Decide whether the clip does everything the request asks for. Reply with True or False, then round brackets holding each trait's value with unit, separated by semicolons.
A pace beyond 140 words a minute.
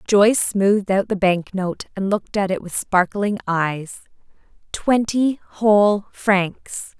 False (135 wpm)